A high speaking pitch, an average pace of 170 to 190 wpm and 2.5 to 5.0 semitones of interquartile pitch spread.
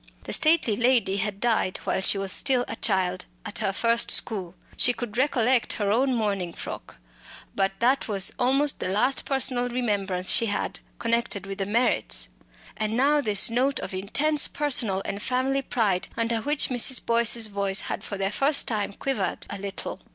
Yes: high, 225 Hz; average, 175 wpm; average, 4.3 semitones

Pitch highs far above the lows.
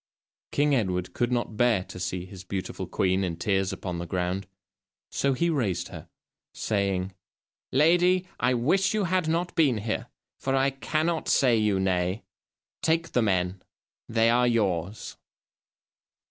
Yes: wide, 6.9 semitones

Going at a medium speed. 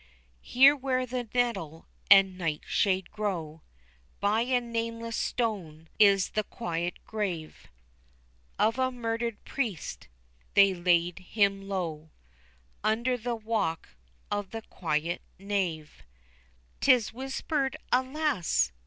No: slow, 105 wpm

